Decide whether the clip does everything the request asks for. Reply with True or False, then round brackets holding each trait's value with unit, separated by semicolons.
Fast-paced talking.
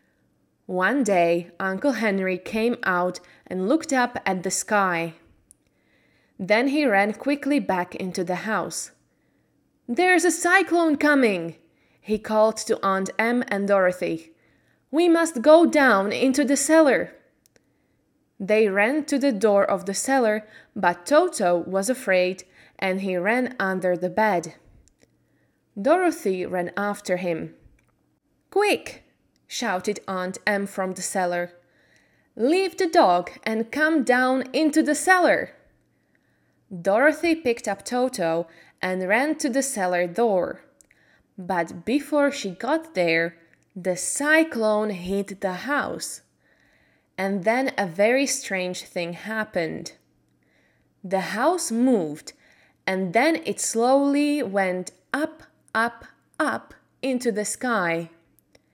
False (120 wpm)